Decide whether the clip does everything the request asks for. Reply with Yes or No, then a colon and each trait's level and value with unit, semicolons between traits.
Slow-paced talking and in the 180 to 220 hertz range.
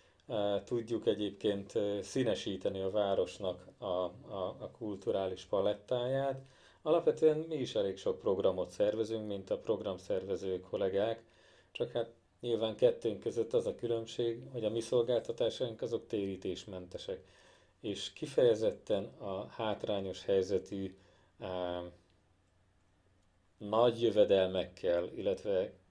No: slow, 100 wpm; low, 115 Hz